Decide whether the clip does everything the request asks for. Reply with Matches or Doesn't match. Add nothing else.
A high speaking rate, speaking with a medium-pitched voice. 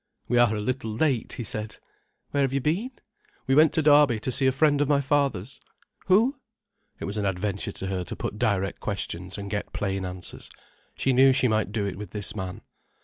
Doesn't match